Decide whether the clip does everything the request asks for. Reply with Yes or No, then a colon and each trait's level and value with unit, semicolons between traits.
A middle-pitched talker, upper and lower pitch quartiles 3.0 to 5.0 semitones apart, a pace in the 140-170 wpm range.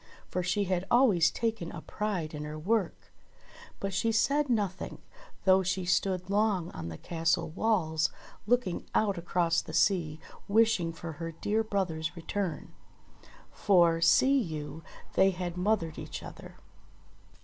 Yes: medium, 180 Hz; average, 3.9 semitones; average, 145 wpm